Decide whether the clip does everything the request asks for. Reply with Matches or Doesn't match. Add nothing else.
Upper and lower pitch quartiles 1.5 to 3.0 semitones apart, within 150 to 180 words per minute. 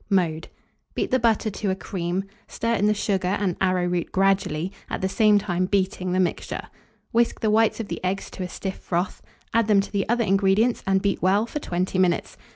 Doesn't match